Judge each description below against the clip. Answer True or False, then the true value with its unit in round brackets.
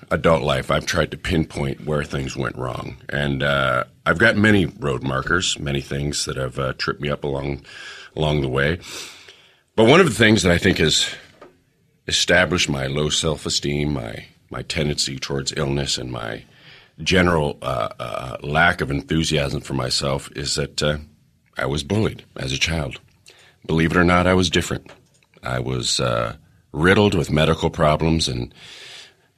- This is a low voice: True (75 Hz)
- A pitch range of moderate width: True (3.1 semitones)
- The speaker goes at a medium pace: True (165 wpm)